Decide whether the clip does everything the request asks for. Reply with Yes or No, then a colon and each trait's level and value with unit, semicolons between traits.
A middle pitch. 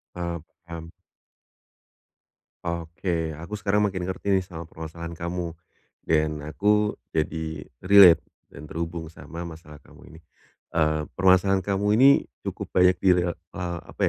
No: very low, 85 Hz